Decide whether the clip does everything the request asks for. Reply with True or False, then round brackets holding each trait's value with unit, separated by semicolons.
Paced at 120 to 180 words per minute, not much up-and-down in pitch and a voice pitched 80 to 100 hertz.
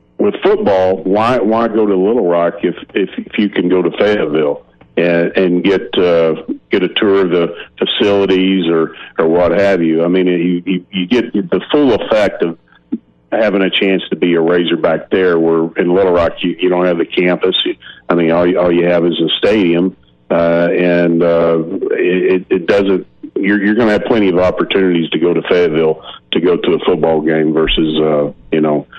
False (200 wpm; 2.3 semitones; 85 Hz)